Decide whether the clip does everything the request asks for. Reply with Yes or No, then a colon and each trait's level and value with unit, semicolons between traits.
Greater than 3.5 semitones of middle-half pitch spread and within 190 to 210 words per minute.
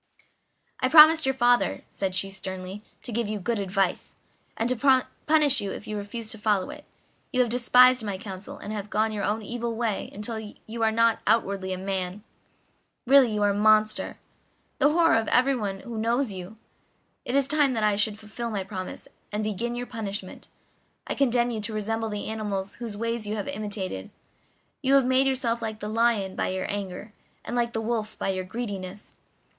No: average, 2.9 semitones; average, 195 wpm